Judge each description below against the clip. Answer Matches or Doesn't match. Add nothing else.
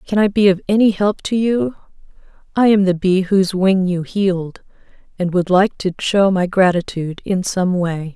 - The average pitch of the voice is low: Doesn't match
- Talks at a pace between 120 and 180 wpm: Doesn't match